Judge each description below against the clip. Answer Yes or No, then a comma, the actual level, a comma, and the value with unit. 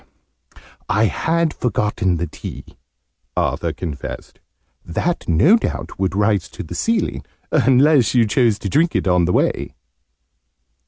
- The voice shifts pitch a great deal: Yes, wide, 8.4 semitones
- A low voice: Yes, low, 105 Hz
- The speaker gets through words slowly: Yes, slow, 130 wpm